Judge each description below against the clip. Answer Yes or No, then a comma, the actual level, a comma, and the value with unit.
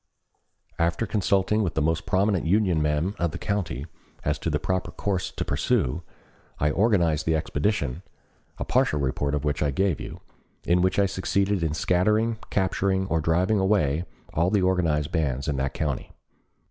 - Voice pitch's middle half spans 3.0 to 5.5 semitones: Yes, average, 4.5 semitones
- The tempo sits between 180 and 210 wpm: No, average, 170 wpm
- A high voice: No, very low, 85 Hz